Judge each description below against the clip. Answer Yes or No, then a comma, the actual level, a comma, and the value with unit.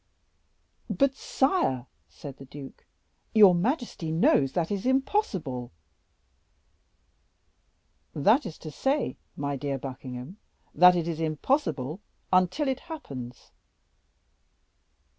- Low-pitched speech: No, medium, 165 Hz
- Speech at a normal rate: No, slow, 105 wpm